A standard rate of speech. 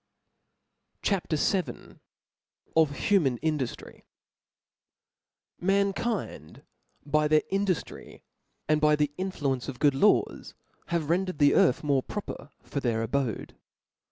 No: slow, 110 wpm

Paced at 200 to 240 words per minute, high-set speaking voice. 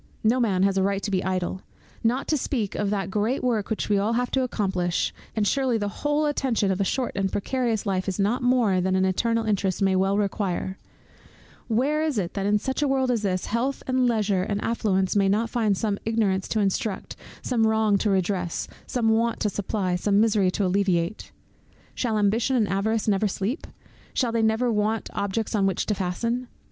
Yes: fast, 205 wpm; high, 210 Hz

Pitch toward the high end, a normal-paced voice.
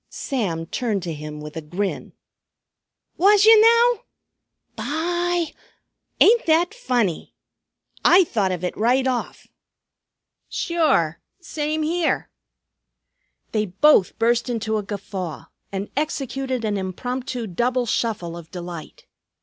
No: high, 240 Hz; slow, 115 wpm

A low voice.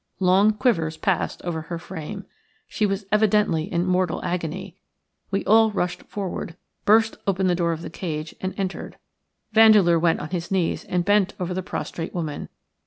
No: medium, 185 Hz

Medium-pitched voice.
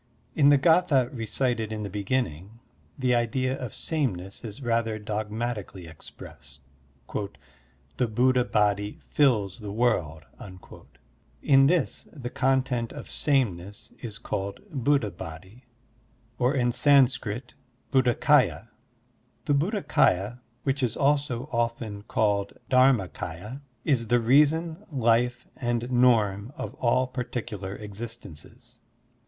No: low, 120 Hz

